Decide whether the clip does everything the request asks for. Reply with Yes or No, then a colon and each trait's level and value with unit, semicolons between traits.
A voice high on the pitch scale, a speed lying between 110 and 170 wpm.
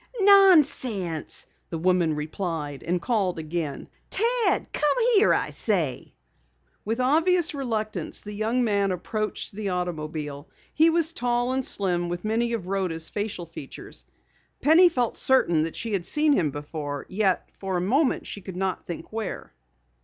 Yes: high, 200 Hz; average, 150 wpm